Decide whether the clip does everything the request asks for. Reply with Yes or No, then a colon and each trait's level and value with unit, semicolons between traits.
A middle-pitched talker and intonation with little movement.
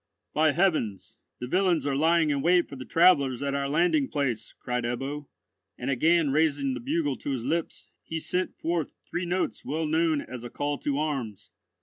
No: medium, 145 Hz; average, 3.7 semitones